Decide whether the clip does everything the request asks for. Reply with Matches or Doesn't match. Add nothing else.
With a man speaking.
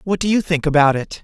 Matches